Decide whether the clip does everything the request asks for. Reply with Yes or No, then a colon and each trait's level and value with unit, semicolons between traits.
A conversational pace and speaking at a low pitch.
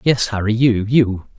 Yes: average, 175 wpm; low, 115 Hz